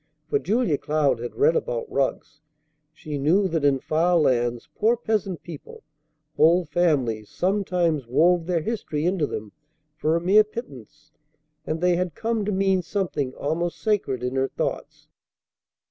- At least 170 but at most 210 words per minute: No, average, 150 wpm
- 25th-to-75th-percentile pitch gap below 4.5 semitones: No, average, 5.3 semitones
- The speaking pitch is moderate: Yes, medium, 170 Hz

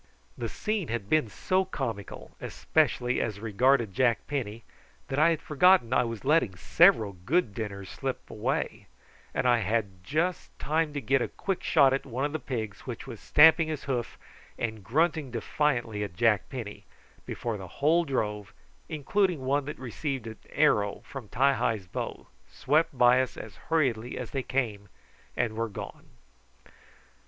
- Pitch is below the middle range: Yes, low, 125 Hz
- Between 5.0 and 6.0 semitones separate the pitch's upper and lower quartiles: Yes, wide, 5.4 semitones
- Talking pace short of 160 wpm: No, average, 165 wpm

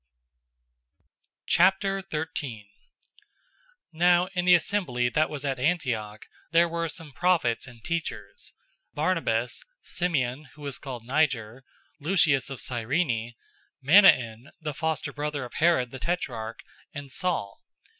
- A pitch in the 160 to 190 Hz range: No, medium, 145 Hz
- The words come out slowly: Yes, slow, 115 wpm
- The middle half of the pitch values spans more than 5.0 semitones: Yes, wide, 5.5 semitones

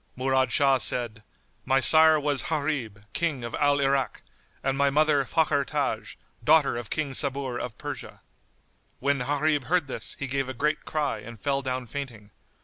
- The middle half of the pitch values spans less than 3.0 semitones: Yes, narrow, 2.5 semitones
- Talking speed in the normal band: Yes, average, 165 wpm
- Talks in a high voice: No, medium, 140 Hz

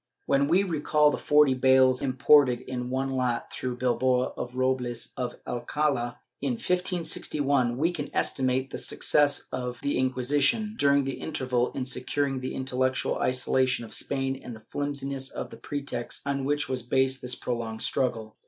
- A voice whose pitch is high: No, low, 130 Hz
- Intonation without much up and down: Yes, narrow, 2.1 semitones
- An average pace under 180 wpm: Yes, average, 165 wpm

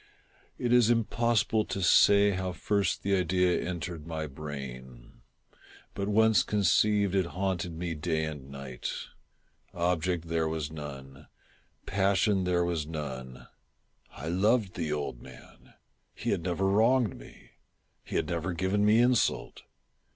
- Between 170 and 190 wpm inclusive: No, slow, 135 wpm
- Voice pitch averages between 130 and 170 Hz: No, very low, 90 Hz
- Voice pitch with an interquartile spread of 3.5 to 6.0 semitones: Yes, average, 4.7 semitones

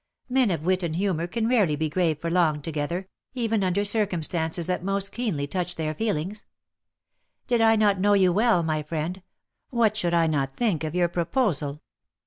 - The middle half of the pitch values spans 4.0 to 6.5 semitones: Yes, average, 4.6 semitones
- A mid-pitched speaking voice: Yes, medium, 180 Hz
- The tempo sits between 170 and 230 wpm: Yes, average, 180 wpm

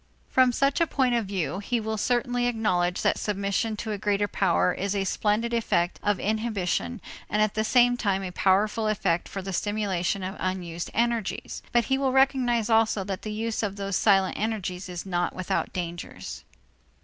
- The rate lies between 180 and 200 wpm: Yes, average, 185 wpm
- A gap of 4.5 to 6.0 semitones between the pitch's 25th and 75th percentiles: No, average, 3.4 semitones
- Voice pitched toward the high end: Yes, high, 205 Hz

